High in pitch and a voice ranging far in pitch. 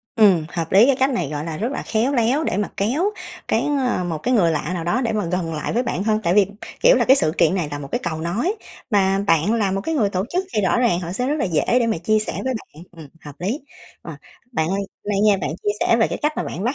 Yes: high, 200 Hz; wide, 5.9 semitones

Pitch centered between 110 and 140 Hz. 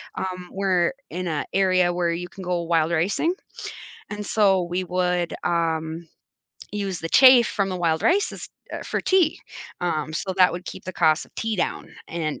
No: medium, 180 Hz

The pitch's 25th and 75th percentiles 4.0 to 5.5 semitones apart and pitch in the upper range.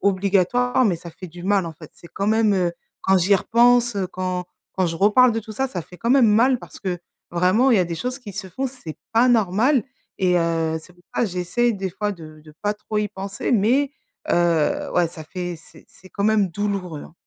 Yes: average, 4.3 semitones; high, 195 Hz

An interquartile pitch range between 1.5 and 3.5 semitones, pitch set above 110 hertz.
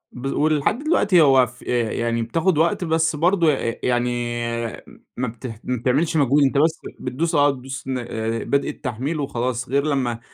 No: average, 4.2 semitones; low, 135 Hz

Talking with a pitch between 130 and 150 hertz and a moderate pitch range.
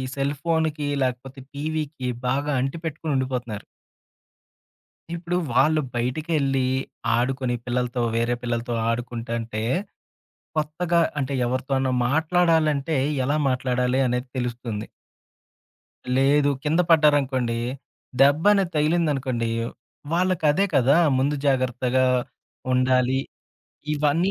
Yes: low, 135 Hz; average, 3.6 semitones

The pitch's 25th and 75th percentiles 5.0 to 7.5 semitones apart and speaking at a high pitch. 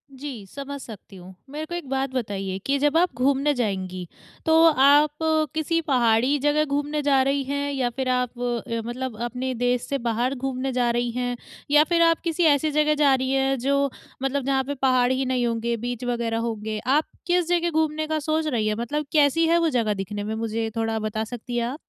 No: average, 3.8 semitones; very high, 265 Hz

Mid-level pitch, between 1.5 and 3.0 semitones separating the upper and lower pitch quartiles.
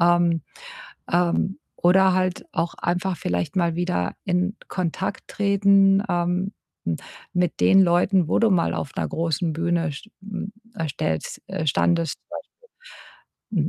Yes: medium, 175 Hz; narrow, 2.4 semitones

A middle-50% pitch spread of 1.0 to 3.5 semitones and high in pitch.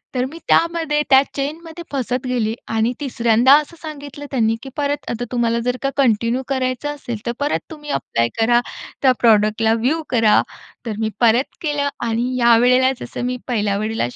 No: average, 3.9 semitones; very high, 250 Hz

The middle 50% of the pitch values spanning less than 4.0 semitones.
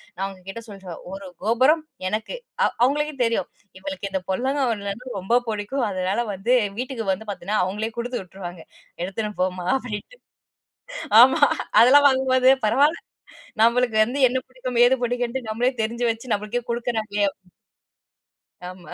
No: average, 4.4 semitones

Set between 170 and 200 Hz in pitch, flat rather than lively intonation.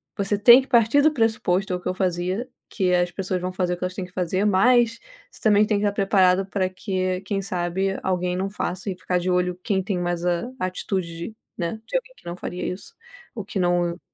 Yes: medium, 185 Hz; narrow, 2.3 semitones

